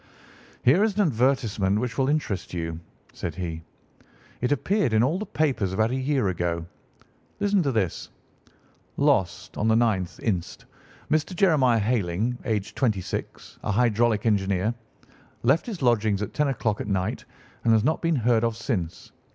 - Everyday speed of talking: Yes, average, 160 wpm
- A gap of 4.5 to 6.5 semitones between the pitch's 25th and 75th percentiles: Yes, wide, 5.5 semitones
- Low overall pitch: Yes, low, 115 Hz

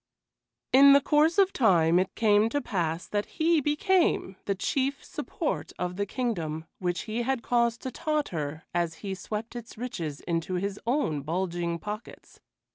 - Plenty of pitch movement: Yes, wide, 7.3 semitones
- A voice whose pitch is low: No, high, 210 Hz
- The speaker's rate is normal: Yes, average, 160 wpm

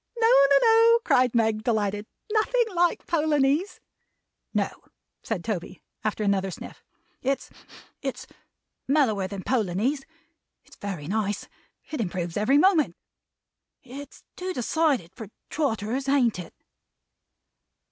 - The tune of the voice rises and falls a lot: Yes, wide, 6.6 semitones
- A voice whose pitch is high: Yes, high, 245 Hz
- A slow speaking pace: Yes, slow, 115 wpm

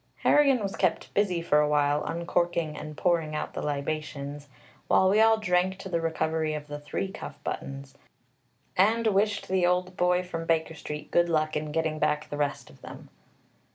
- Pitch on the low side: No, medium, 165 Hz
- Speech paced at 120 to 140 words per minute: No, average, 185 wpm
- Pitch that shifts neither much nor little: Yes, average, 3.5 semitones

